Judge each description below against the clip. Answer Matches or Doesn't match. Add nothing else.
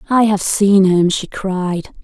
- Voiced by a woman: Matches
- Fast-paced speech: Doesn't match